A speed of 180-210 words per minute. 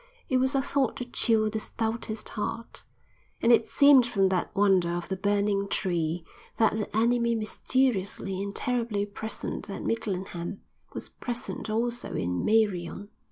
No: average, 150 wpm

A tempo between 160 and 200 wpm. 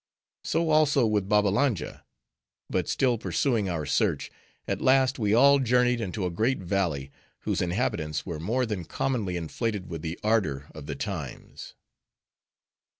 No: average, 145 wpm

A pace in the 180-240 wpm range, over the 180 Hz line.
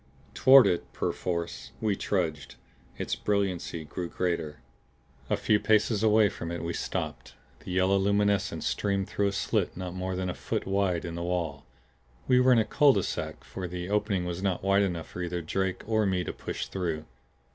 No: average, 190 wpm; very low, 95 Hz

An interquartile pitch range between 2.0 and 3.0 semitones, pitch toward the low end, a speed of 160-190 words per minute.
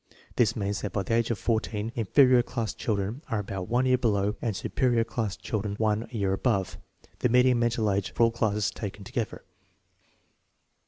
Yes: average, 2.7 semitones; low, 110 Hz; average, 175 wpm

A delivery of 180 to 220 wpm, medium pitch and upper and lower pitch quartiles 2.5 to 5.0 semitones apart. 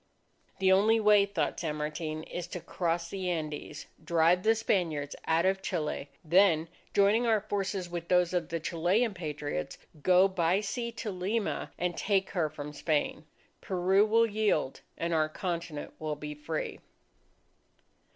No: average, 150 wpm; medium, 175 Hz; average, 3.9 semitones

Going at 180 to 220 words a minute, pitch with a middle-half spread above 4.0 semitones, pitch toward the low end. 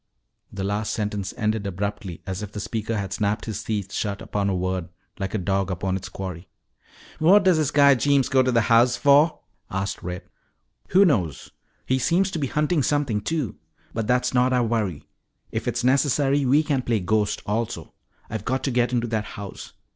Yes: average, 190 wpm; average, 5.3 semitones; low, 110 Hz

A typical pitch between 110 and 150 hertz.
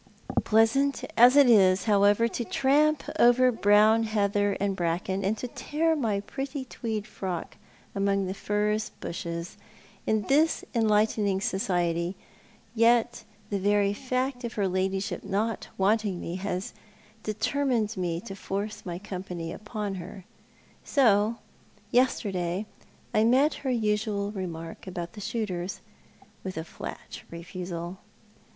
No: high, 205 Hz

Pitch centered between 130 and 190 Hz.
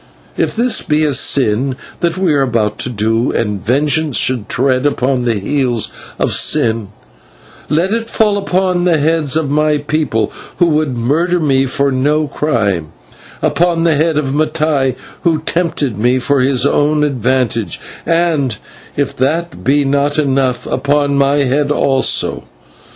Yes: medium, 140 Hz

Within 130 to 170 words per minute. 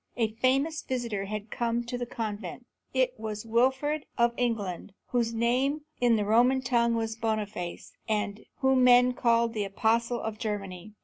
Yes: average, 160 wpm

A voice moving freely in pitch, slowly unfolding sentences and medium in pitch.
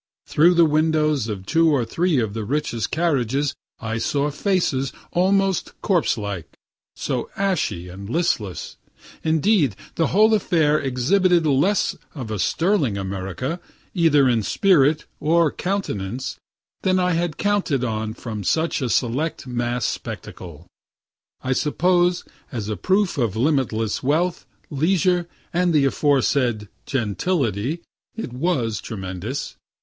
Yes: wide, 7.2 semitones; slow, 125 wpm; medium, 145 Hz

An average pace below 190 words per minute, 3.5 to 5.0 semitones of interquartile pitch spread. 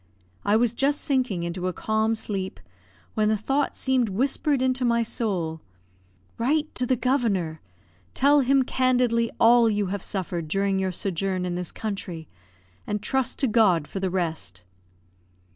No: average, 155 wpm; wide, 5.4 semitones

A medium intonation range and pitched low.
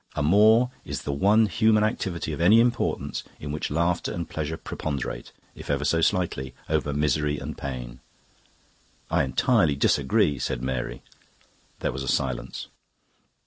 No: wide, 6.3 semitones; very low, 75 Hz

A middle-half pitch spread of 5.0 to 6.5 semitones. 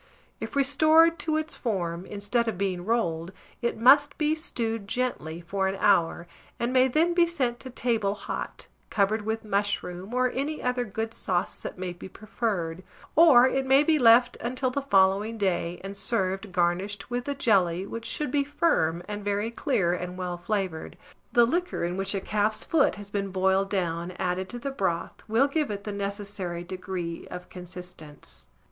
Yes: average, 5.3 semitones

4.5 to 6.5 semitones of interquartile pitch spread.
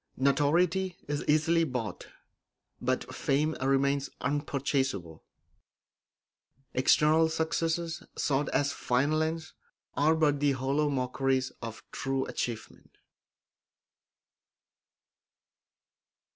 No: average, 3.0 semitones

